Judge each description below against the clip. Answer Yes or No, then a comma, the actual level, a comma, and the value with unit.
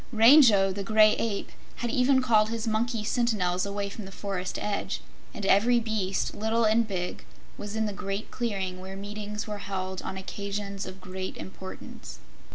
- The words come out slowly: No, average, 165 wpm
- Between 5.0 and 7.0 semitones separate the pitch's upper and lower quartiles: No, narrow, 2.4 semitones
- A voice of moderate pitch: No, high, 205 Hz